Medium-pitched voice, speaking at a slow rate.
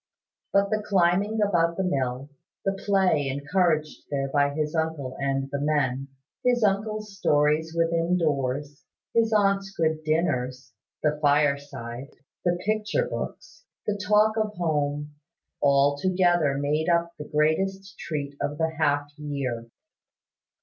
Yes: medium, 155 Hz; slow, 130 wpm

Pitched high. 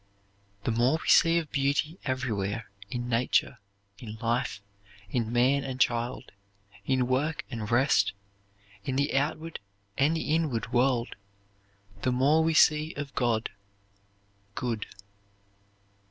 No: low, 130 Hz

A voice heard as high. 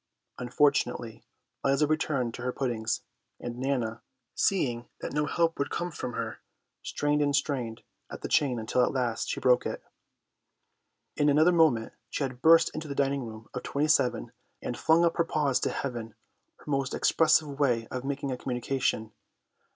No: low, 135 Hz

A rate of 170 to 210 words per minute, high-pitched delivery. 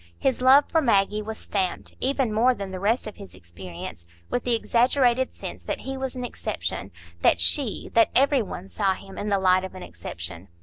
Yes: average, 200 wpm; high, 210 Hz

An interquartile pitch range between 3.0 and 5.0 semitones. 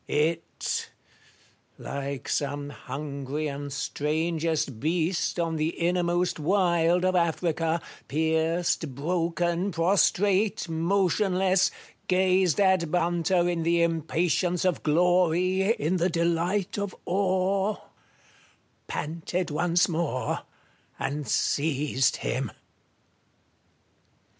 No: narrow, 2.6 semitones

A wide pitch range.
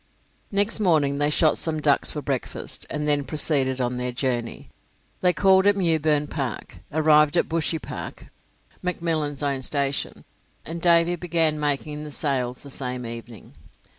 No: average, 3.4 semitones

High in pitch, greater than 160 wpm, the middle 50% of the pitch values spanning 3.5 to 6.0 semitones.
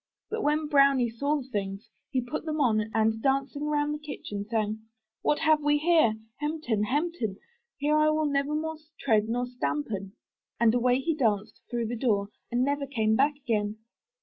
Yes: very high, 260 Hz; average, 180 wpm; average, 5.2 semitones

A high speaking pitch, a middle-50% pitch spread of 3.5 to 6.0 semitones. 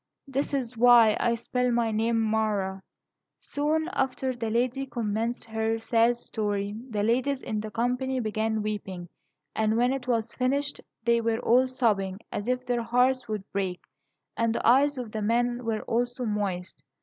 No: high, 230 Hz; average, 2.7 semitones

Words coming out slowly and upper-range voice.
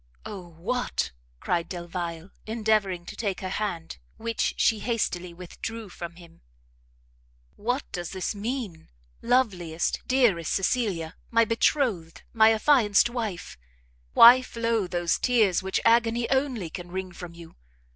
Yes: slow, 125 wpm; high, 200 Hz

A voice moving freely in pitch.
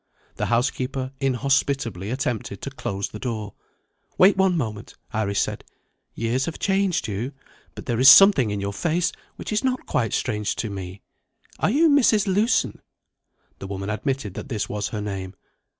Yes: wide, 7.9 semitones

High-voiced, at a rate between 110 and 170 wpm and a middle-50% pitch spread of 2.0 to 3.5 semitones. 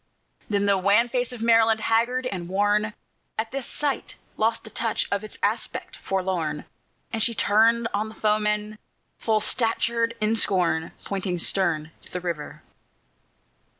Yes: high, 215 Hz; average, 150 wpm; average, 3.0 semitones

